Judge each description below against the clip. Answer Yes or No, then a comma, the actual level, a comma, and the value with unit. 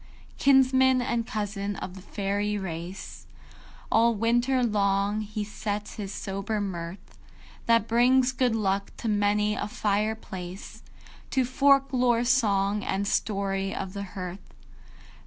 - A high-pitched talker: Yes, high, 210 Hz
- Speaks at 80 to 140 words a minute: Yes, slow, 135 wpm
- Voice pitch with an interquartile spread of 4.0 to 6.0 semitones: No, average, 3.1 semitones